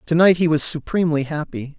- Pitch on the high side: No, medium, 155 Hz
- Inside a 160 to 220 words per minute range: Yes, average, 200 wpm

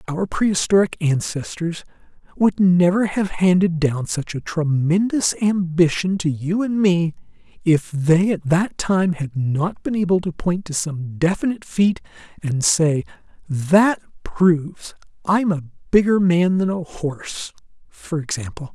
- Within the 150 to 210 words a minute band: No, average, 140 wpm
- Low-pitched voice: No, medium, 175 Hz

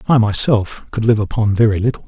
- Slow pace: No, fast, 205 wpm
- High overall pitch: No, low, 110 Hz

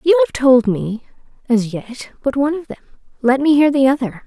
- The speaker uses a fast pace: No, average, 195 wpm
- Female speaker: Yes, female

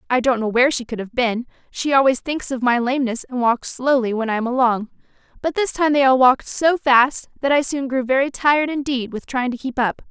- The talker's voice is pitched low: No, very high, 255 Hz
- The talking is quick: Yes, fast, 245 wpm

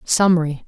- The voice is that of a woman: Yes, female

